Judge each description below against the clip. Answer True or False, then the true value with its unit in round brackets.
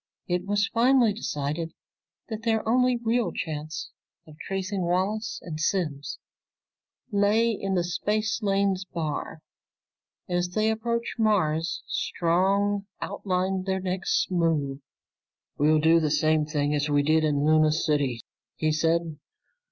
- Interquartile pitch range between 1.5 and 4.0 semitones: False (4.7 semitones)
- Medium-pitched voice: True (180 Hz)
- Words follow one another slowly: True (125 wpm)